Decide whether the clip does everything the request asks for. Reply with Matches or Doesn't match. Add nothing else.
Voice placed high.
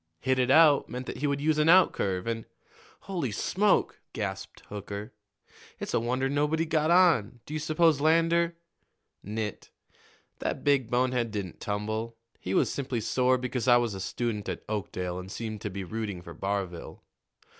Doesn't match